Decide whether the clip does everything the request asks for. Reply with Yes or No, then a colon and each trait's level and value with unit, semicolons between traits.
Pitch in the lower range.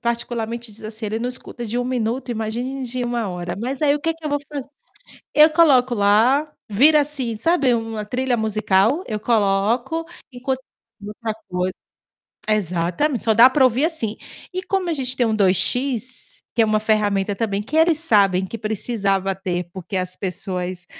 No: high, 230 Hz